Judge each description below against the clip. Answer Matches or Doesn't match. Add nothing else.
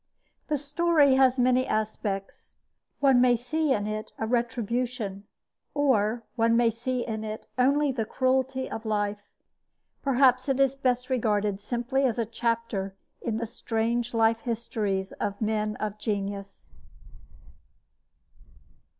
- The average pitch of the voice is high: Matches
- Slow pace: Matches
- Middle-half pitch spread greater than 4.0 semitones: Doesn't match